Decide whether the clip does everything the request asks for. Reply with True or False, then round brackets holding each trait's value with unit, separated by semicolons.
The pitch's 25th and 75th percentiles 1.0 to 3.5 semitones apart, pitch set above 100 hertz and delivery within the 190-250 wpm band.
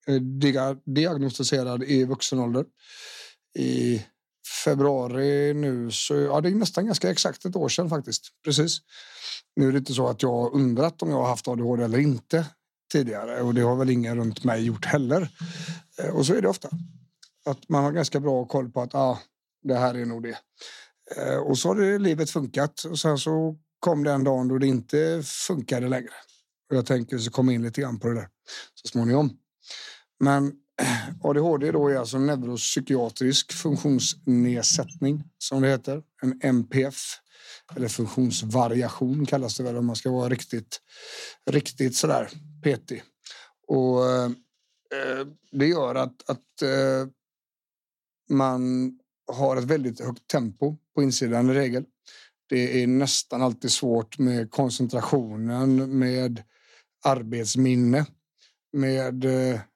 False (2.8 semitones; 135 Hz; 150 wpm)